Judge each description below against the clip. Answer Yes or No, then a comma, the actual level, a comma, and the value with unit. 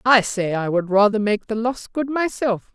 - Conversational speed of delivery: No, fast, 220 wpm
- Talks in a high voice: Yes, high, 220 Hz